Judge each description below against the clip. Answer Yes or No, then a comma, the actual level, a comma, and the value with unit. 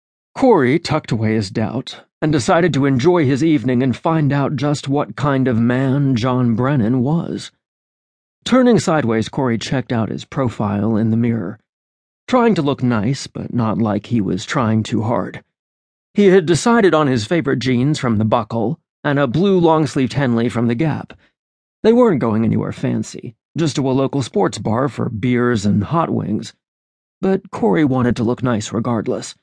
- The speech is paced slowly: No, average, 175 wpm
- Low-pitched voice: Yes, low, 130 Hz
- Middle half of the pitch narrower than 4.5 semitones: No, average, 5.2 semitones